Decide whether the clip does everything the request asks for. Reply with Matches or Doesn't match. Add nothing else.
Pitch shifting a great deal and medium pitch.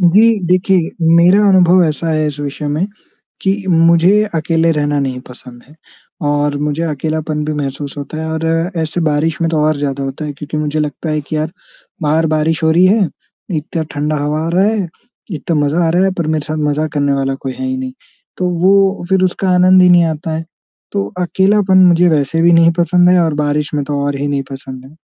Doesn't match